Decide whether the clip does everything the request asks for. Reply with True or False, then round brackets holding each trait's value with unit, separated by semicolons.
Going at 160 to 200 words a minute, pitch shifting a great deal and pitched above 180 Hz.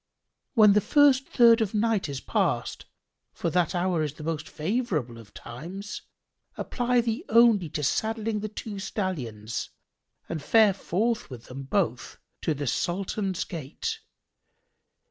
False (145 wpm; 6.8 semitones; 190 Hz)